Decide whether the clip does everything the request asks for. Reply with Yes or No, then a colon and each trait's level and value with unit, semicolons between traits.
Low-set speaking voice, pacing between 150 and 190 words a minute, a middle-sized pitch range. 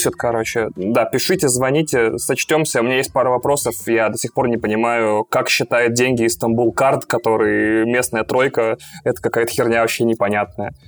No: low, 115 Hz; fast, 160 wpm; narrow, 2.2 semitones